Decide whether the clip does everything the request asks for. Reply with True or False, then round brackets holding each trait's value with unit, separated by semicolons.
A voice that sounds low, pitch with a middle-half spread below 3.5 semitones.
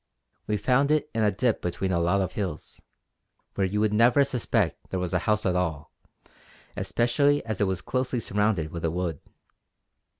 False (105 Hz; 4.8 semitones)